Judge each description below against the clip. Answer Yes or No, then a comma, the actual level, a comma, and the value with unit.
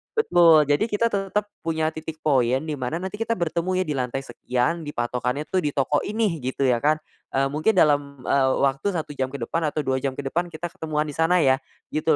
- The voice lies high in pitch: No, medium, 155 Hz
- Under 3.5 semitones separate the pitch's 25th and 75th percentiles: No, average, 4.0 semitones